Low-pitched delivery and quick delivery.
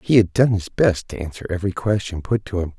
Yes: low, 100 Hz; fast, 260 wpm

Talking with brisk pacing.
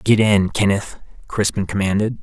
No: slow, 135 wpm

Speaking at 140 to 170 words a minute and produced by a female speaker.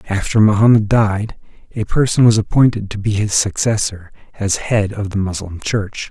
No: average, 165 wpm; male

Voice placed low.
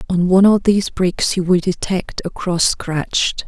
No: medium, 185 Hz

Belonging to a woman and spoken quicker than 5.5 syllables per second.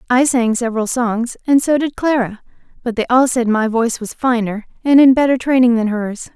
No: female; 5.4 syllables/s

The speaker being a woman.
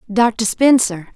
Yes: female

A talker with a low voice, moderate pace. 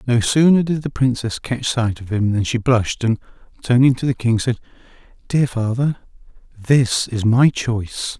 Yes: low, 120 Hz; average, 175 wpm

